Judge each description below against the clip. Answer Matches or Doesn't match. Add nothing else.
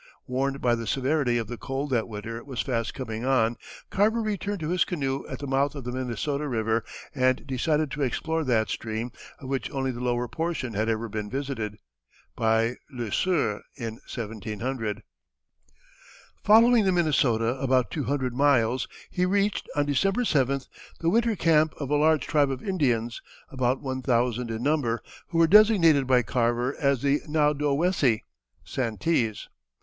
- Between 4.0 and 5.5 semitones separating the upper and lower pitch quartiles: Matches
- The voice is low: Matches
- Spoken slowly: Doesn't match